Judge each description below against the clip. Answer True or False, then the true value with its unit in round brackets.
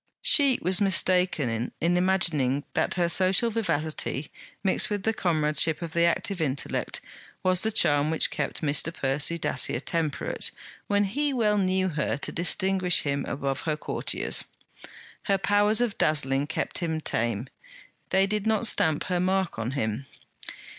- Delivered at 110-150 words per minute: True (145 wpm)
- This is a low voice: False (170 Hz)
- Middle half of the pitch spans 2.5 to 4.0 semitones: False (4.9 semitones)